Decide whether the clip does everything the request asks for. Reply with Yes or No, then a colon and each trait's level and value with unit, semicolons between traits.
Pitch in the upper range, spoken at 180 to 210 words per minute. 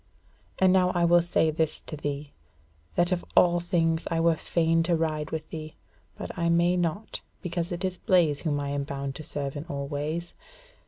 No: medium, 165 Hz; average, 200 wpm